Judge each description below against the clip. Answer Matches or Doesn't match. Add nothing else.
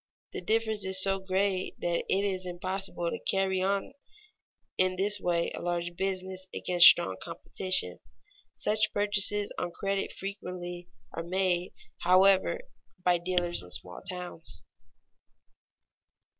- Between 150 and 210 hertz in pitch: Matches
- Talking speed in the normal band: Doesn't match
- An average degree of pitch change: Doesn't match